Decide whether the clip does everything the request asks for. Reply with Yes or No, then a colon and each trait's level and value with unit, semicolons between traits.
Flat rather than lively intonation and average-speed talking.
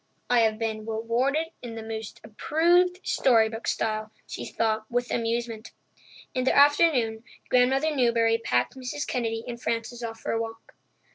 Yes: narrow, 2.3 semitones; average, 145 wpm